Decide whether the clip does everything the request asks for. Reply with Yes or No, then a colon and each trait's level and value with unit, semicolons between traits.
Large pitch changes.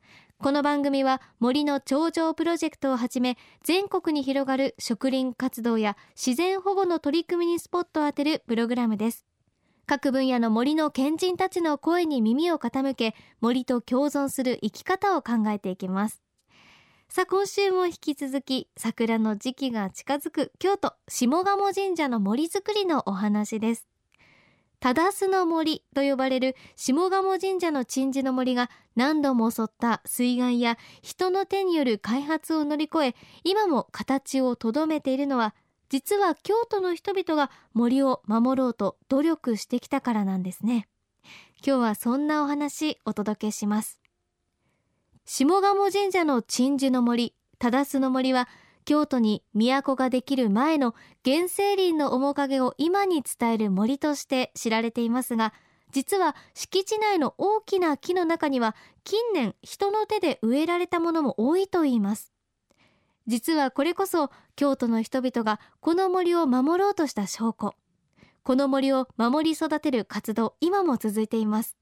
Yes: wide, 5.7 semitones